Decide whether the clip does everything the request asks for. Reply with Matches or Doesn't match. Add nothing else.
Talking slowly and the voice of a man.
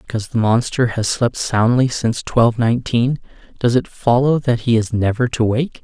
Doesn't match